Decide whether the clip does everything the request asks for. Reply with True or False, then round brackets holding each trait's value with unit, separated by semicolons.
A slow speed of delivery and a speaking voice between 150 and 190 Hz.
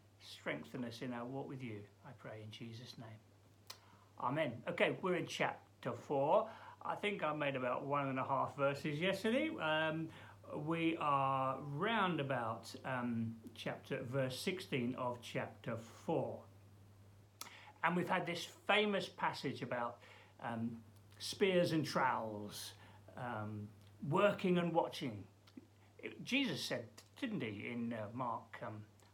False (130 wpm; 125 Hz)